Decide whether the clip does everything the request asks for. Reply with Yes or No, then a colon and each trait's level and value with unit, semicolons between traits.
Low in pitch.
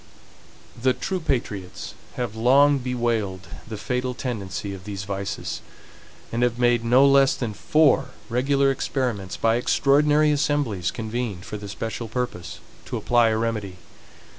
Yes: low, 120 Hz